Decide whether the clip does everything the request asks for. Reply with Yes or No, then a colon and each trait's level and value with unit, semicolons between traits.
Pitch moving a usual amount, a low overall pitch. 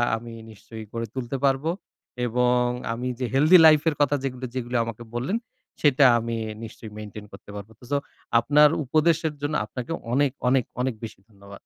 Yes: average, 4.0 semitones; low, 125 Hz